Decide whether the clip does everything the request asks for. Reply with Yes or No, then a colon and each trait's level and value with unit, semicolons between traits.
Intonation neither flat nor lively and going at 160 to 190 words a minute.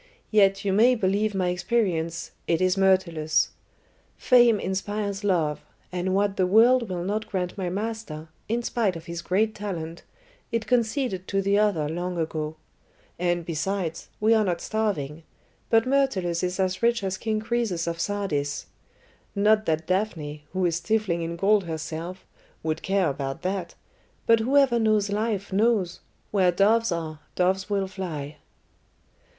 No: average, 4.0 semitones; average, 150 wpm